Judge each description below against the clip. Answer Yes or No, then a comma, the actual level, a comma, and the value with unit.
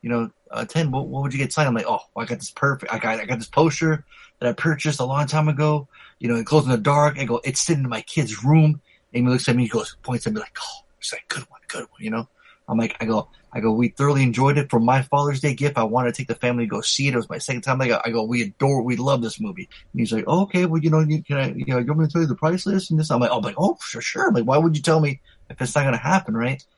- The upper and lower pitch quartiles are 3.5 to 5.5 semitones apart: Yes, average, 4.2 semitones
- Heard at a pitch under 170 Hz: Yes, low, 135 Hz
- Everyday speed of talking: No, fast, 340 wpm